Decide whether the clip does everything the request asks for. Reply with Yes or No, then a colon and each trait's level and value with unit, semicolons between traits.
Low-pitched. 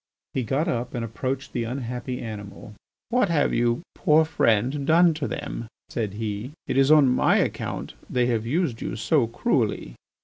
Yes: low, 125 Hz